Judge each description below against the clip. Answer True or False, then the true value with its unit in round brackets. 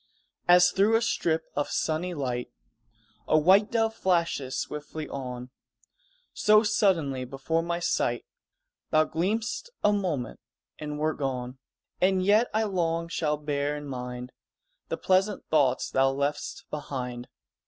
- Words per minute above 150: False (135 wpm)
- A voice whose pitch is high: False (155 Hz)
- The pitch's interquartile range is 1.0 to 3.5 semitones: False (5.6 semitones)